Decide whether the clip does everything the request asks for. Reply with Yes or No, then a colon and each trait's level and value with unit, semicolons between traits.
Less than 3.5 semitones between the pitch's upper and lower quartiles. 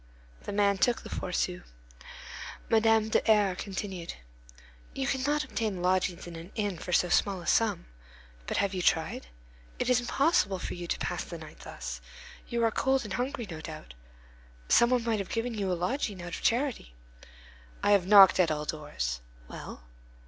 No: average, 4.6 semitones